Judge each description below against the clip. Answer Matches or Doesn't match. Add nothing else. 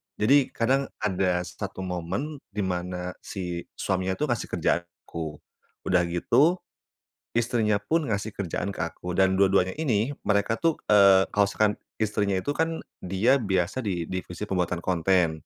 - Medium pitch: Doesn't match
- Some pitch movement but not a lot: Matches